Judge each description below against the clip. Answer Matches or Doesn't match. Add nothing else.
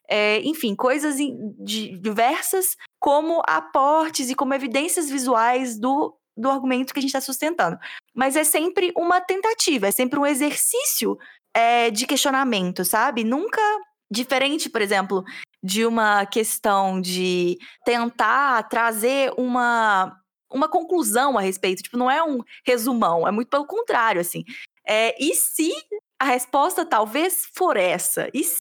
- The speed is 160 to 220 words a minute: Doesn't match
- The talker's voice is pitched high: Matches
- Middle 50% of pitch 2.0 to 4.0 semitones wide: Doesn't match